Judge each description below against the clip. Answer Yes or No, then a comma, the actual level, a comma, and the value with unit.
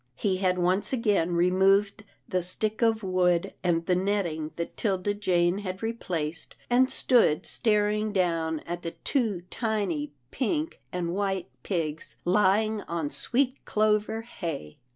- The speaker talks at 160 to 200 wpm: No, slow, 135 wpm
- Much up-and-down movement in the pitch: No, average, 3.7 semitones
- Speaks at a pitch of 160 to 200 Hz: Yes, high, 190 Hz